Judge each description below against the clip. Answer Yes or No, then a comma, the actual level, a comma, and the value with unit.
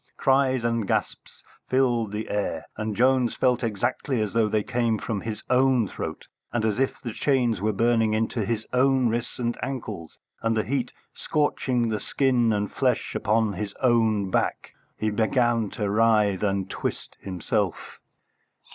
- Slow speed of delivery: No, average, 160 wpm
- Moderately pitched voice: No, low, 115 Hz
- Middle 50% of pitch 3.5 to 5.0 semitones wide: No, average, 2.8 semitones